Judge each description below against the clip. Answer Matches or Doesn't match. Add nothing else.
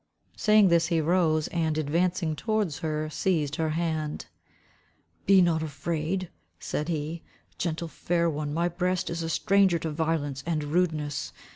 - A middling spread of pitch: Doesn't match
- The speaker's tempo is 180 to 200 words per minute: Doesn't match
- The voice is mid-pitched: Matches